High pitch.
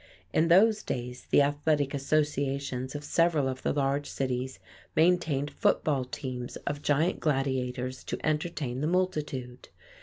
No: medium, 140 Hz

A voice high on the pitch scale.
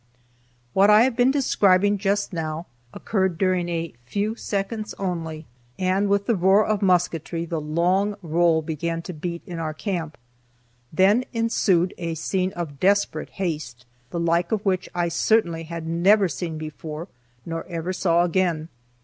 No: medium, 175 Hz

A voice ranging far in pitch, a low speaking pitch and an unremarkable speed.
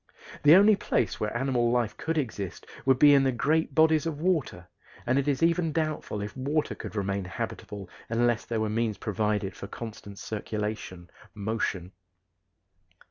Yes: wide, 6.1 semitones; low, 120 Hz; average, 160 wpm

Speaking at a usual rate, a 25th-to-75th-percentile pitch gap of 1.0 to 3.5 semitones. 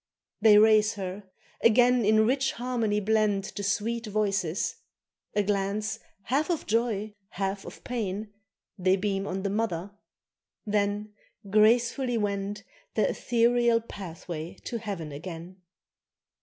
No: slow, 120 wpm; narrow, 2.6 semitones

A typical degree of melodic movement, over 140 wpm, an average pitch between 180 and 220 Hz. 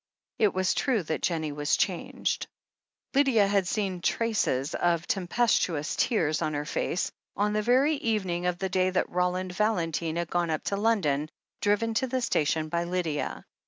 Yes: average, 4.5 semitones; average, 170 wpm; medium, 185 Hz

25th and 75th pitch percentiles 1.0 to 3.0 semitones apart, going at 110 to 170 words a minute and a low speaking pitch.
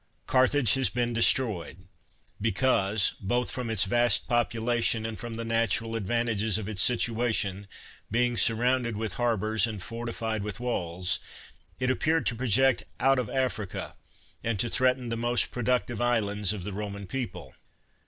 Yes: narrow, 2.6 semitones; average, 150 wpm; low, 115 Hz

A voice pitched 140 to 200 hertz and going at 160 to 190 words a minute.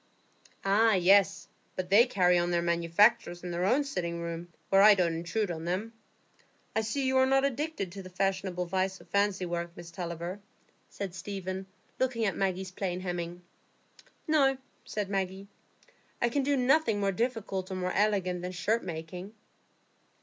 Yes: high, 190 Hz; average, 165 wpm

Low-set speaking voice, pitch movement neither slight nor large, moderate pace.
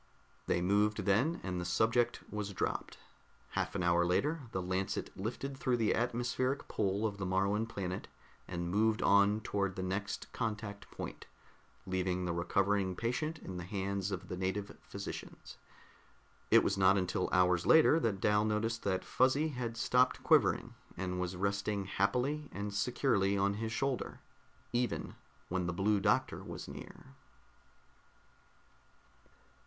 Yes: low, 100 Hz; average, 3.6 semitones; average, 145 wpm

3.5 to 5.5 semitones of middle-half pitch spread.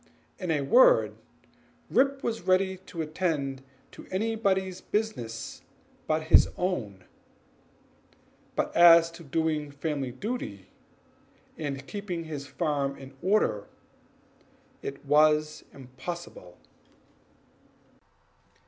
Yes: average, 5.2 semitones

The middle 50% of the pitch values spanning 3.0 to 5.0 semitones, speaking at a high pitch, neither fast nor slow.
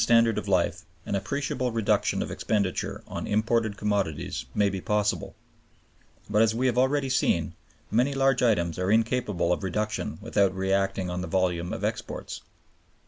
No: average, 3.5 semitones; low, 105 Hz; average, 170 wpm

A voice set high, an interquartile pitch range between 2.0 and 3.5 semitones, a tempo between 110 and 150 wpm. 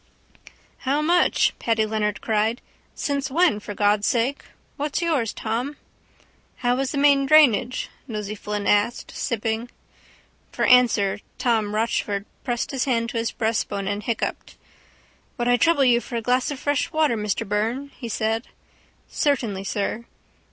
No: high, 235 Hz; average, 4.2 semitones; average, 145 wpm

